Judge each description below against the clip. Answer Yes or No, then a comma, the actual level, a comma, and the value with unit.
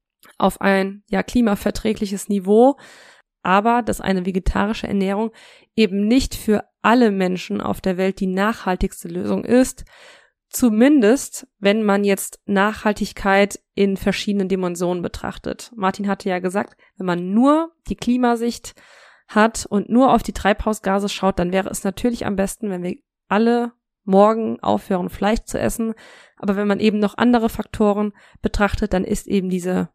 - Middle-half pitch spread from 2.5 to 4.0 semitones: Yes, average, 2.8 semitones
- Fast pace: No, average, 145 wpm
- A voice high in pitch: Yes, high, 205 Hz